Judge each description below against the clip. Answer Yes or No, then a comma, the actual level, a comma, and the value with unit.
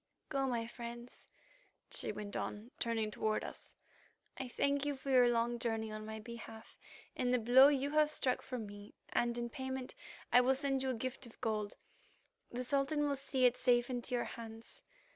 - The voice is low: No, high, 245 Hz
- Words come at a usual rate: Yes, average, 185 wpm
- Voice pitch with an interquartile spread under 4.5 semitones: Yes, narrow, 2.6 semitones